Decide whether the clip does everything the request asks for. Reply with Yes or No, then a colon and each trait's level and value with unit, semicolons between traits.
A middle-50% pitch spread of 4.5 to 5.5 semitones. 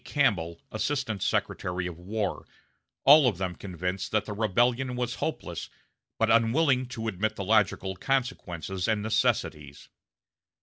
Yes: average, 5.2 semitones